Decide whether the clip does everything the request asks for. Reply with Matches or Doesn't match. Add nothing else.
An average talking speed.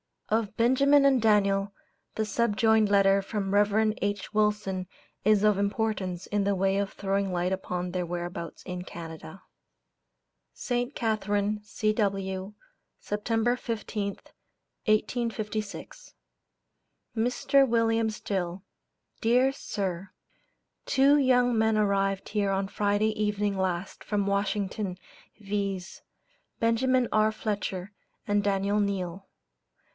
Doesn't match